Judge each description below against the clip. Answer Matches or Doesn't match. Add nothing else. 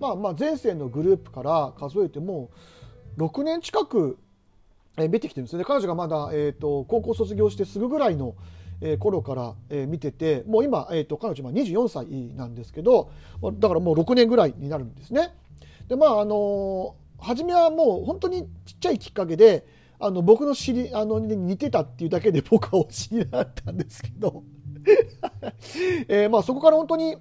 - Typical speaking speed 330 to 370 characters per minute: Doesn't match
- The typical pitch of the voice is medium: Matches